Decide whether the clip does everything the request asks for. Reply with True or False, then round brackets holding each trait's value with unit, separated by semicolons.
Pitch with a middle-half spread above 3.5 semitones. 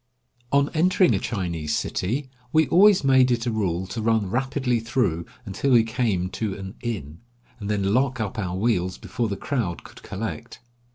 True (5.2 semitones)